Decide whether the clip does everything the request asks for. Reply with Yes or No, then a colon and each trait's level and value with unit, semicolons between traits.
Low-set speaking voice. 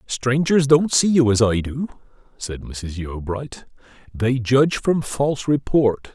Yes: low, 125 Hz